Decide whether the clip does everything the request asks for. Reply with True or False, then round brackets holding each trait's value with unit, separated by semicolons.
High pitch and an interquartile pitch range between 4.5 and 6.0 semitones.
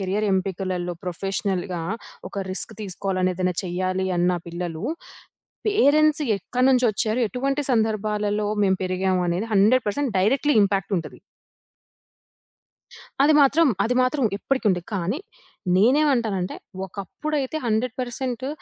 True (205 Hz; 5.5 semitones)